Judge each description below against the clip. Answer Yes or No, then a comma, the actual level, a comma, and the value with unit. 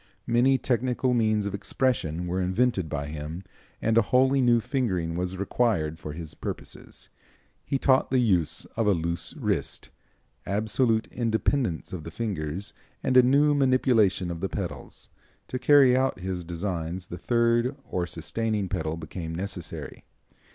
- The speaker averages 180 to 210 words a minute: No, average, 150 wpm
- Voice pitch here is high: No, low, 100 Hz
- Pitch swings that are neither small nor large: No, wide, 6.2 semitones